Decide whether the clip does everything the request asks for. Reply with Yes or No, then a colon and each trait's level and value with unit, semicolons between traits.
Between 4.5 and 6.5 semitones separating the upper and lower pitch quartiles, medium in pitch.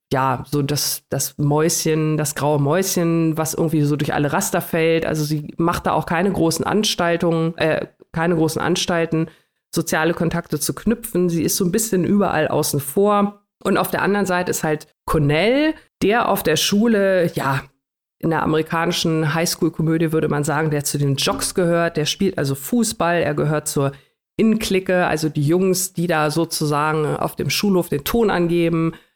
No: average, 3.1 semitones; medium, 165 Hz